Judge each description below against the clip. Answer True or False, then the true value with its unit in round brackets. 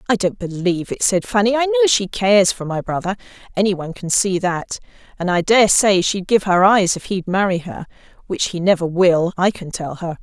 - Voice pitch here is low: False (195 Hz)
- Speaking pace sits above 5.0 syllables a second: True (5.4 syllables/s)